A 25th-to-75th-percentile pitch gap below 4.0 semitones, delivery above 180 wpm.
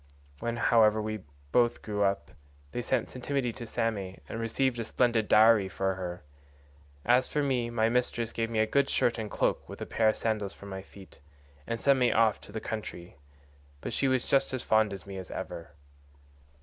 Yes: average, 3.0 semitones; average, 200 wpm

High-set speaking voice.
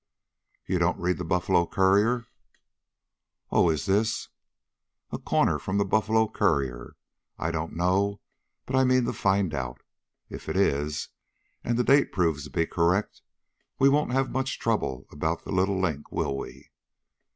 No: very low, 95 Hz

